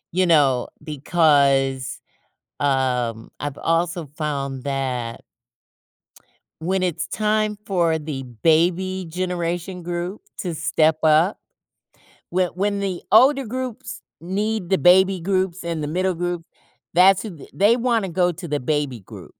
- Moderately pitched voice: Yes, medium, 175 Hz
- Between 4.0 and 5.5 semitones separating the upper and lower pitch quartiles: Yes, average, 4.4 semitones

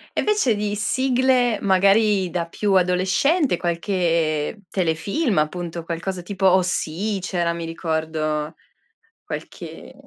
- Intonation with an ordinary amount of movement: Yes, average, 3.7 semitones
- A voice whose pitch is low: No, medium, 185 Hz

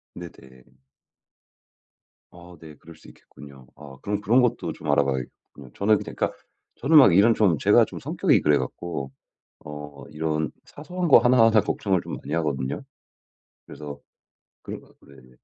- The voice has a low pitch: Yes, very low, 80 Hz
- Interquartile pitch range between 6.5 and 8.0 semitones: Yes, wide, 6.8 semitones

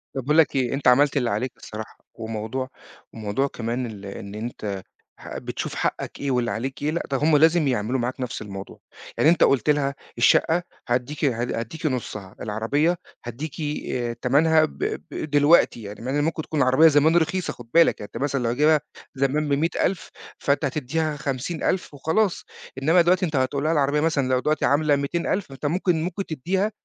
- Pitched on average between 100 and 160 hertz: Yes, medium, 140 Hz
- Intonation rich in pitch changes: No, average, 4.3 semitones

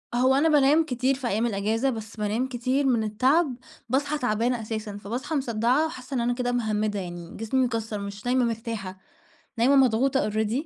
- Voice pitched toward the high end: Yes, high, 240 Hz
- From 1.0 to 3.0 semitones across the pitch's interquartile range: No, average, 3.5 semitones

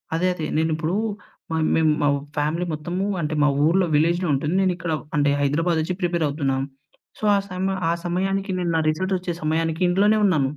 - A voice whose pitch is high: No, medium, 170 Hz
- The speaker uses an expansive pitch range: No, average, 2.8 semitones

